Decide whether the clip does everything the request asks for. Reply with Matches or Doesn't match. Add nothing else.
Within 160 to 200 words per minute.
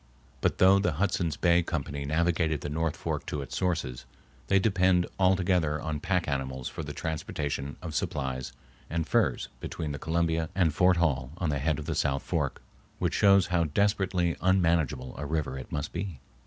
Matches